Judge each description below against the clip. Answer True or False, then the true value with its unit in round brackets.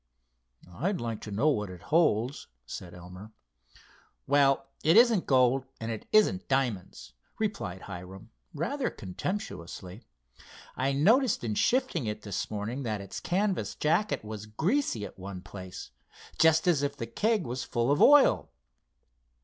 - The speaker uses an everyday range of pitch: False (8.6 semitones)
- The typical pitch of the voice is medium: False (125 Hz)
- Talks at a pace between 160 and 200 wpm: False (140 wpm)